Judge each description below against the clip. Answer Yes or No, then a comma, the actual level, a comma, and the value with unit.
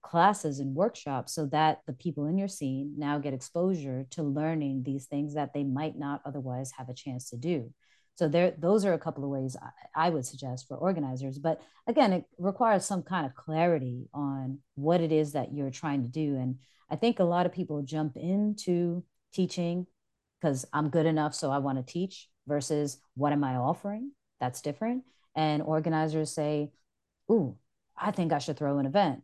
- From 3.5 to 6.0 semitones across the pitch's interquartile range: Yes, average, 4.0 semitones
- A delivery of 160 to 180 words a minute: No, average, 195 wpm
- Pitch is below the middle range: No, medium, 150 Hz